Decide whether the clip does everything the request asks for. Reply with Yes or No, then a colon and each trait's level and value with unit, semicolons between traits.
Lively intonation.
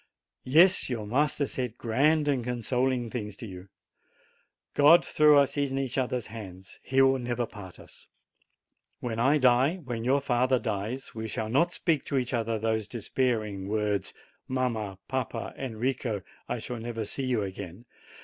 No: average, 3.4 semitones